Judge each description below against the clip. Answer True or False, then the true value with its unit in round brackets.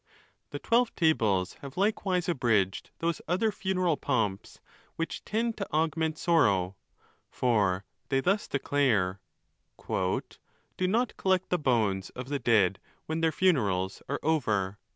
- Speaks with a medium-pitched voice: True (145 Hz)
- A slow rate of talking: True (130 wpm)